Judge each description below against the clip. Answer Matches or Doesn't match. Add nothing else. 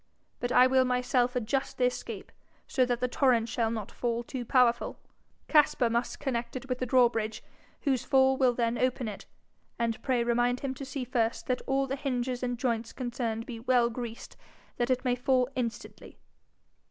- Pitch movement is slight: Matches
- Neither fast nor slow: Matches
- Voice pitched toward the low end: Doesn't match